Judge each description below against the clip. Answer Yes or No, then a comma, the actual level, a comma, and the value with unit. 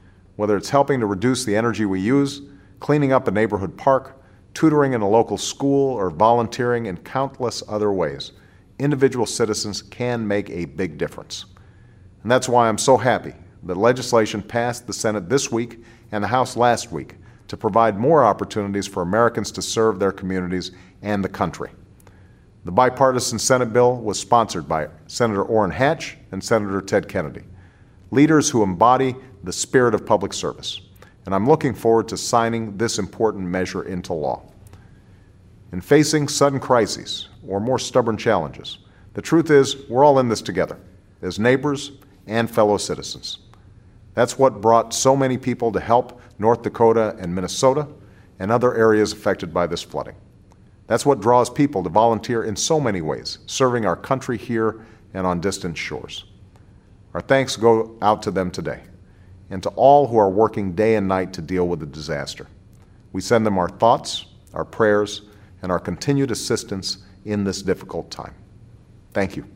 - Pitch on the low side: Yes, low, 105 Hz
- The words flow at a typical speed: Yes, average, 165 wpm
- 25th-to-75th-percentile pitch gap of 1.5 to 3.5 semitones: No, average, 4.2 semitones